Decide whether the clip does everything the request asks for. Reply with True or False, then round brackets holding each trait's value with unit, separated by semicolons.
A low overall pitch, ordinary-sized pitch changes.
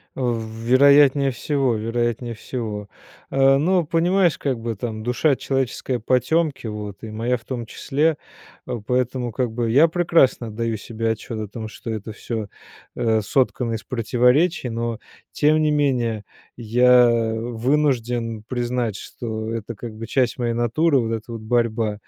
True (120 Hz; 3.0 semitones)